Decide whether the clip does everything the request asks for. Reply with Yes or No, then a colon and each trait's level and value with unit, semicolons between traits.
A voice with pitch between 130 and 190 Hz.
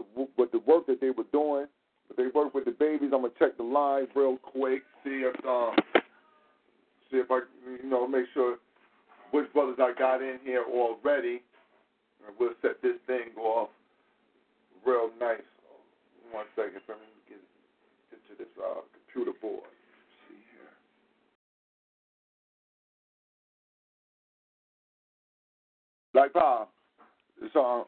Yes: low, 135 Hz